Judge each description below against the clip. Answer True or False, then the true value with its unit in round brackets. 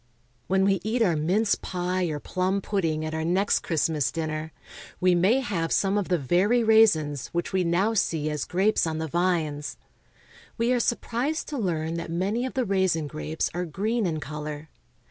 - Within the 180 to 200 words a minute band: True (185 wpm)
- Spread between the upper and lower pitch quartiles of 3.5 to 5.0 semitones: True (4.4 semitones)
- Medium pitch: True (180 Hz)